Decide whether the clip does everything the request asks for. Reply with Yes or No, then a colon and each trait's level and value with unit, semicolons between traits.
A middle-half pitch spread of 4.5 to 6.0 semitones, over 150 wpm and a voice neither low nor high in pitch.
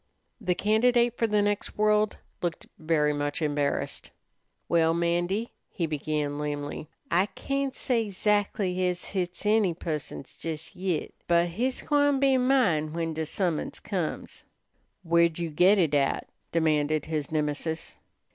No: average, 5.1 semitones; slow, 135 wpm; medium, 170 Hz